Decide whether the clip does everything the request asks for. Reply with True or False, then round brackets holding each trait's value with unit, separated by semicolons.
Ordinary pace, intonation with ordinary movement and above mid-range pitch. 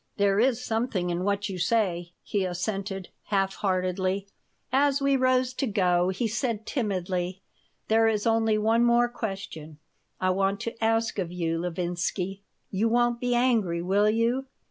True (155 wpm; 3.9 semitones; 205 Hz)